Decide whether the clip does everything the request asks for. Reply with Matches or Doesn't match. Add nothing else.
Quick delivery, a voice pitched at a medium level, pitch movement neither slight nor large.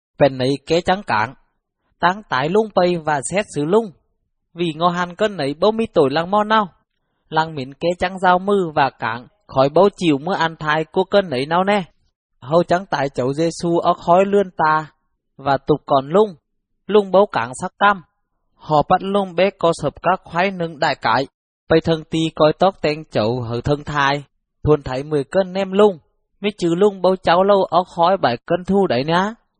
Doesn't match